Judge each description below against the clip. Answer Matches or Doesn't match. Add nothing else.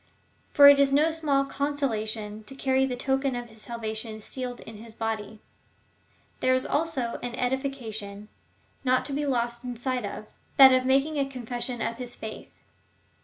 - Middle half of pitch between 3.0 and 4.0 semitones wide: Matches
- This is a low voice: Doesn't match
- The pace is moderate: Matches